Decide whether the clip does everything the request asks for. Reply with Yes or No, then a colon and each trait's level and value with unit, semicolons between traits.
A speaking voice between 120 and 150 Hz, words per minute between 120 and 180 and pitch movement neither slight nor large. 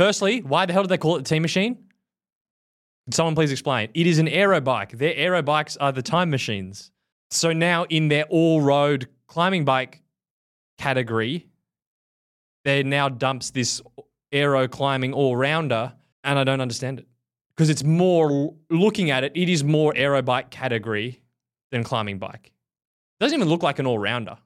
Yes: medium, 140 Hz; average, 170 wpm; average, 4.6 semitones